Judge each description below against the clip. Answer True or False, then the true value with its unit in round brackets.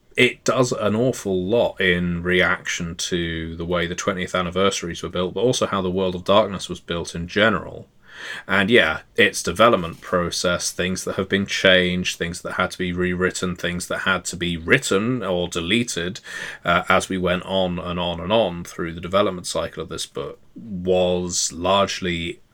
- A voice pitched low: True (90 Hz)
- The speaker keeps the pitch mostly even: True (1.9 semitones)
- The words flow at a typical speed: True (180 wpm)